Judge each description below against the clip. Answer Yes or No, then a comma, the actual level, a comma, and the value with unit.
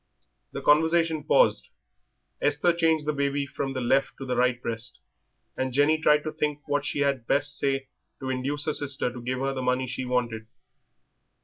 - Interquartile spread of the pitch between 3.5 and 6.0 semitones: No, narrow, 2.6 semitones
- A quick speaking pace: No, average, 185 wpm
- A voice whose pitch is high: No, medium, 140 Hz